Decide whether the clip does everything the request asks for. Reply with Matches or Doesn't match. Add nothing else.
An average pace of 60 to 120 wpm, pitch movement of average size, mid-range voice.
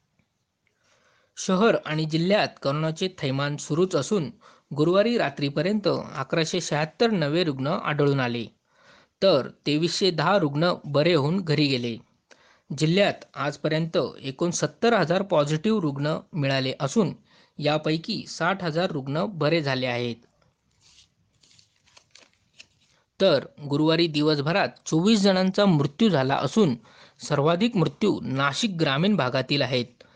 Matches